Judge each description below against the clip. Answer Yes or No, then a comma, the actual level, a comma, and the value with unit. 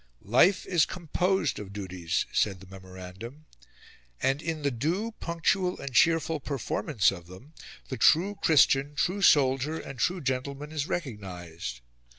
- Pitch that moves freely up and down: Yes, wide, 8.8 semitones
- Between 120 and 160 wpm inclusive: Yes, average, 140 wpm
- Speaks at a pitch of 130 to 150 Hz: Yes, medium, 140 Hz